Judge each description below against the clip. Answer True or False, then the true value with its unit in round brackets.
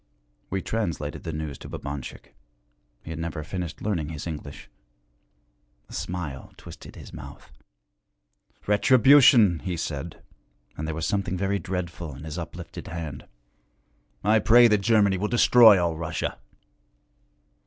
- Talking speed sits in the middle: False (130 wpm)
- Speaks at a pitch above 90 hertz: False (85 Hz)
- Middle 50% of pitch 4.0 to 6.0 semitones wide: True (4.8 semitones)